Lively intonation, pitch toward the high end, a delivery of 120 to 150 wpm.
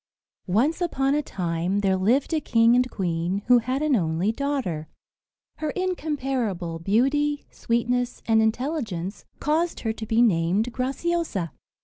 Yes: wide, 6.8 semitones; high, 235 Hz; slow, 135 wpm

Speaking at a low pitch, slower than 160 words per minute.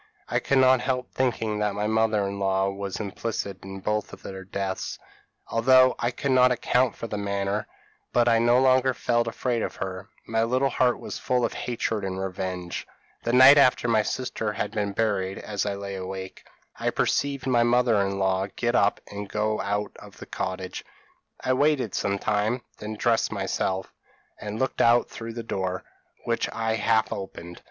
No: low, 110 Hz; average, 180 wpm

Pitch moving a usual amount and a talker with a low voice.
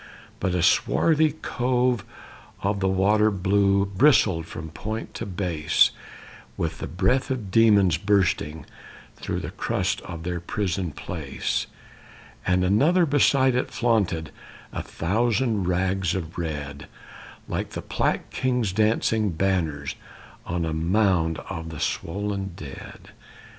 Yes: average, 4.6 semitones; very low, 95 Hz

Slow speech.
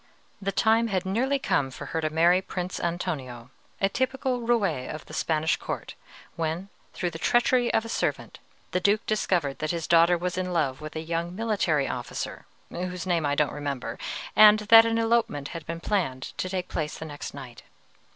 No: average, 190 wpm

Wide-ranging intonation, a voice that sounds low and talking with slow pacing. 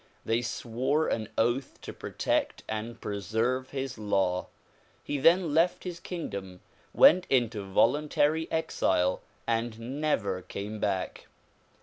Yes: wide, 6.3 semitones; low, 120 Hz; slow, 115 wpm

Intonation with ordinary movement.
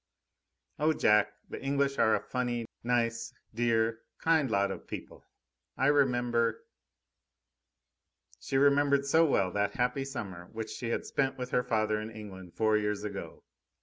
Yes: average, 4.1 semitones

